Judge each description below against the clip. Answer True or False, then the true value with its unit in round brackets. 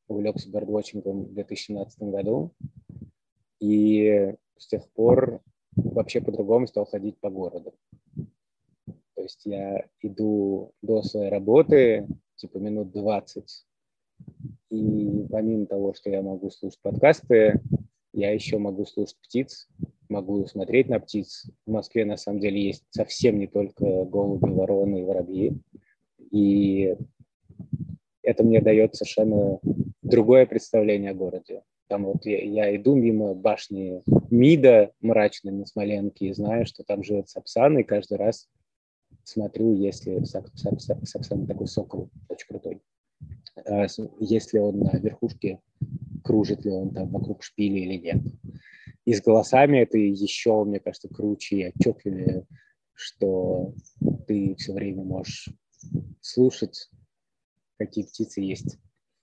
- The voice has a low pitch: True (105 Hz)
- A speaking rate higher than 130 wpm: False (125 wpm)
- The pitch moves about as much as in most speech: False (1.7 semitones)